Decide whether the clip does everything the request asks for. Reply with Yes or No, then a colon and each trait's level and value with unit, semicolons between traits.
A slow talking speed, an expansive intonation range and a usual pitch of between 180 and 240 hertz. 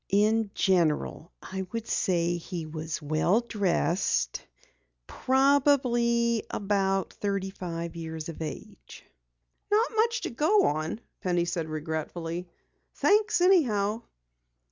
Yes: slow, 105 wpm; wide, 6.0 semitones; high, 190 Hz